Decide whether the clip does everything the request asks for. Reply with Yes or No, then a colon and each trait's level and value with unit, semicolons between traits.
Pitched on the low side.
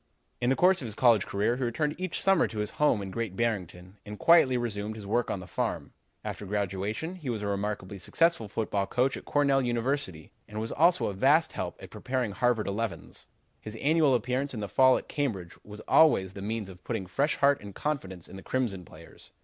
Yes: low, 115 Hz